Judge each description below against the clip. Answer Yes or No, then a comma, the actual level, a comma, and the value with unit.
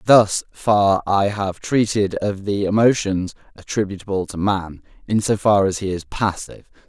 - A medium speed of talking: Yes, average, 155 wpm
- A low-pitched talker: Yes, low, 100 Hz